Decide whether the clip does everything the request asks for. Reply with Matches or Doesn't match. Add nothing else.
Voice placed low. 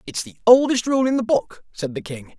Doesn't match